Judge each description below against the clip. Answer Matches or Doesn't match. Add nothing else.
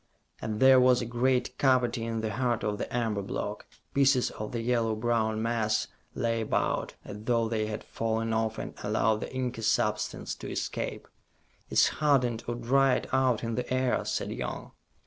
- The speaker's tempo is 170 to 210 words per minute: Matches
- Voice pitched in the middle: Doesn't match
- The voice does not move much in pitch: Matches